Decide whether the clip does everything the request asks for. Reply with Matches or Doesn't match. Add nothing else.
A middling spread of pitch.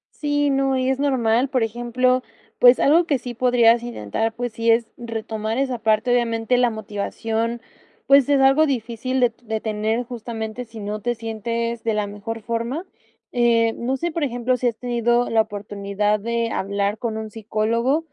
Doesn't match